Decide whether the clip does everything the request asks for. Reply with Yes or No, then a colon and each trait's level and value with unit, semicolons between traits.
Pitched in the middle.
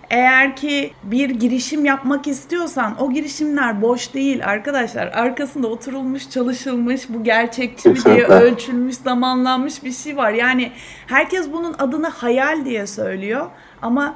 No: very high, 260 Hz